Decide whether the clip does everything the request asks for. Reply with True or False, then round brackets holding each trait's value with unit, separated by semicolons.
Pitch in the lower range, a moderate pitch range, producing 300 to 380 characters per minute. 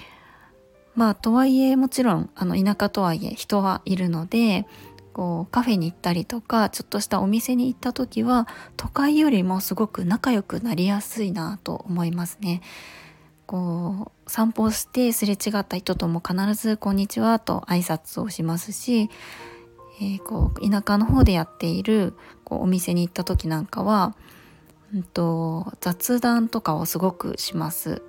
False (200 Hz; 4.5 semitones; 320 characters per minute)